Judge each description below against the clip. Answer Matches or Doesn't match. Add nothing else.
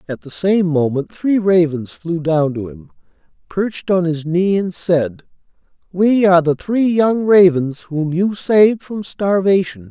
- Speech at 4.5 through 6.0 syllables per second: Doesn't match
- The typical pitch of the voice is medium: Matches